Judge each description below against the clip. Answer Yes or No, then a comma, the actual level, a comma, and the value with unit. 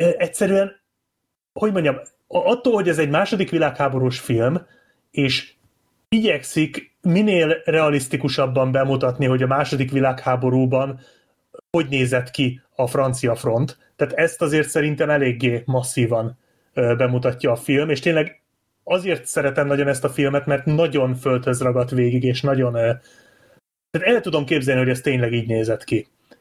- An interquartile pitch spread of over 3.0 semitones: Yes, average, 4.0 semitones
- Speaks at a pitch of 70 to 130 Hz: No, medium, 140 Hz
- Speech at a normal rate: Yes, average, 130 wpm